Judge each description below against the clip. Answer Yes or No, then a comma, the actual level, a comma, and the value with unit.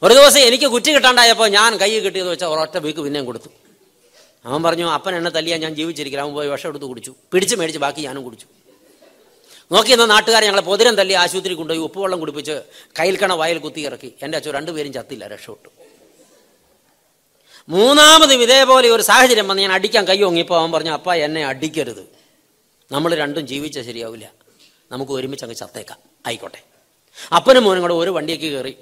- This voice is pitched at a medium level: Yes, medium, 170 Hz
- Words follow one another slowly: No, average, 165 wpm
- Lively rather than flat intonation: Yes, wide, 6.4 semitones